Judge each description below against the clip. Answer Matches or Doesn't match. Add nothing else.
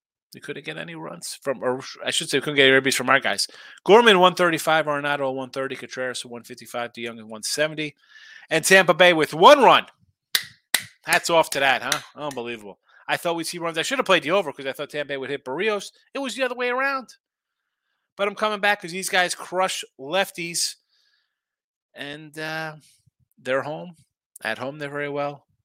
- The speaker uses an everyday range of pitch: Doesn't match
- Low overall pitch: Doesn't match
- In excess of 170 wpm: Matches